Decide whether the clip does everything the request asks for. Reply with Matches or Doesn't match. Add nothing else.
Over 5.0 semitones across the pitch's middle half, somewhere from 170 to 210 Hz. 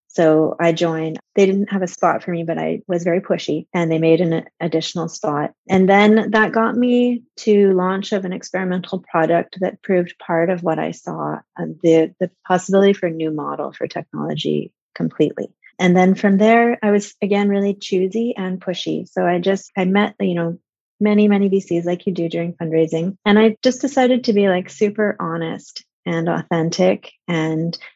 Doesn't match